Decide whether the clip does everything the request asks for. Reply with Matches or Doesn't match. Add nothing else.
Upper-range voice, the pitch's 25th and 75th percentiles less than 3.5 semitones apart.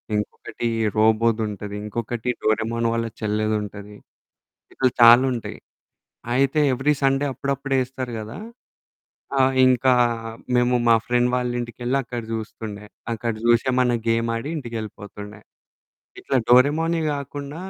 Doesn't match